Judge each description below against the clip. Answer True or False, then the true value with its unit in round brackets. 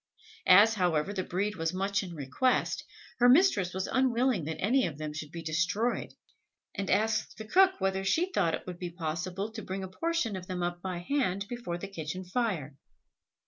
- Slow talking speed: False (190 wpm)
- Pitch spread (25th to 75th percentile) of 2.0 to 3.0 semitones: False (4.2 semitones)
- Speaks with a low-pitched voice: False (190 Hz)